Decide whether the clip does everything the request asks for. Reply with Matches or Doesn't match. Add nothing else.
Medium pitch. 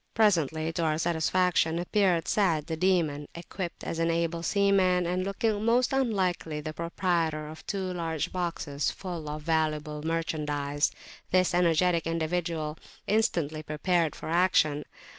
Matches